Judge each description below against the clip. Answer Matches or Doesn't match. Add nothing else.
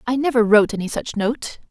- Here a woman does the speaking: Matches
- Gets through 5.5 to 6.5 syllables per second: Matches